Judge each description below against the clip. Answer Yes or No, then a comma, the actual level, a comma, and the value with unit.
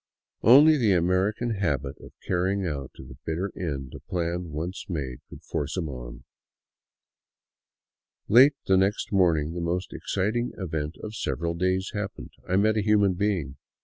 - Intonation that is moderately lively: Yes, average, 4.5 semitones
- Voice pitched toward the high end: No, very low, 90 Hz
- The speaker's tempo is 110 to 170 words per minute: Yes, average, 160 wpm